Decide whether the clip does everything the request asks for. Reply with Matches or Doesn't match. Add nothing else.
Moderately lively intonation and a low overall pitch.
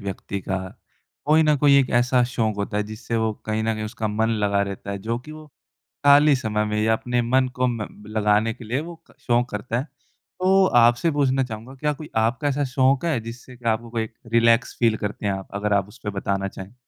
Matches